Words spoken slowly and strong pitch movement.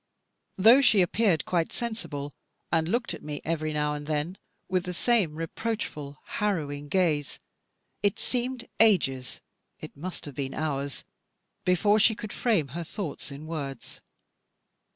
No: average, 150 wpm; wide, 6.0 semitones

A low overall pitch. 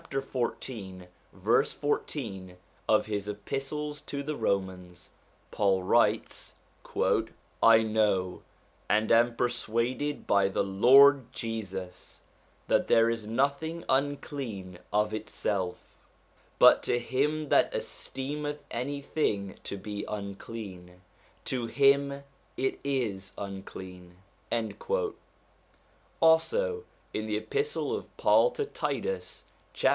Yes: low, 115 Hz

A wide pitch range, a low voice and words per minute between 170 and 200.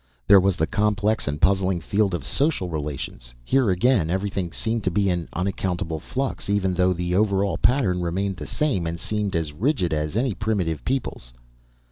No: average, 3.7 semitones; very low, 95 Hz; average, 180 wpm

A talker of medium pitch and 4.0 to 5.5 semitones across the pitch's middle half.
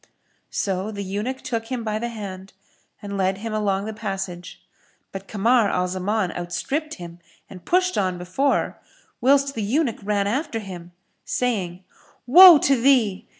No: high, 210 Hz; average, 4.6 semitones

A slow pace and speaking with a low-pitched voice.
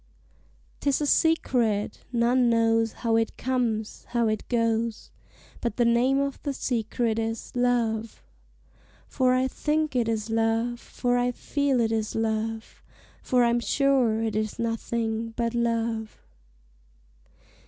No: slow, 130 wpm; high, 230 Hz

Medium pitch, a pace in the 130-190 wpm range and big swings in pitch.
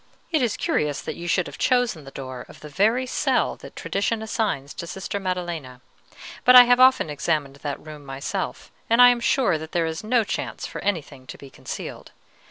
No: medium, 175 Hz; average, 200 wpm; wide, 7.9 semitones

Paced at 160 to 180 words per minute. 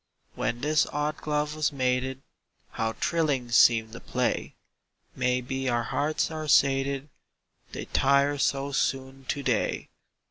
No: slow, 135 wpm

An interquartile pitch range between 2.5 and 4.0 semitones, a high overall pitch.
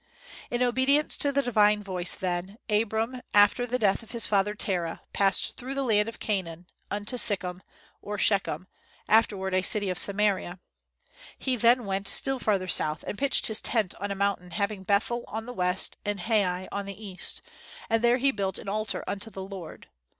Yes: average, 3.1 semitones; high, 205 Hz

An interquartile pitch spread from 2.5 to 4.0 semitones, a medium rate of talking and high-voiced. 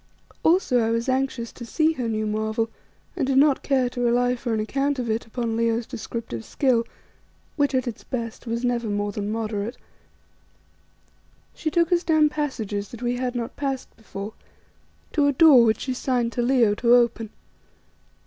Yes: average, 3.0 semitones; average, 175 wpm; high, 240 Hz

